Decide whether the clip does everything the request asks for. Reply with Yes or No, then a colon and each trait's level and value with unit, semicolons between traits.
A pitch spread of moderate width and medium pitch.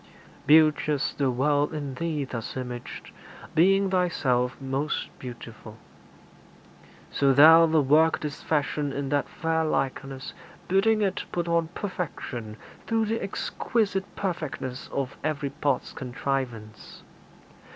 Yes: average, 4.0 semitones; medium, 145 Hz